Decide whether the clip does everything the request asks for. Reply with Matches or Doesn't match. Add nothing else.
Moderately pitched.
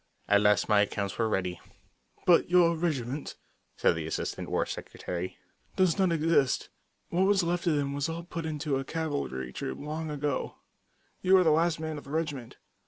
Matches